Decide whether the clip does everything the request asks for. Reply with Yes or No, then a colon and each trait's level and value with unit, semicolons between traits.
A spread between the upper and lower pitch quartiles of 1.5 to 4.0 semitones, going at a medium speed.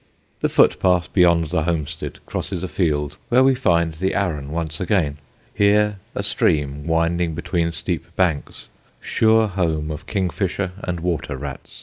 Yes: average, 3.5 semitones; average, 145 wpm